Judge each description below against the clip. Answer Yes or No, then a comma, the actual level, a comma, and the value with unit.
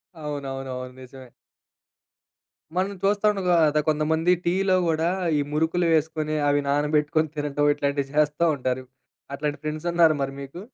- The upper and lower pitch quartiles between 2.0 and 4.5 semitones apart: Yes, narrow, 2.5 semitones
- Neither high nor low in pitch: Yes, medium, 150 Hz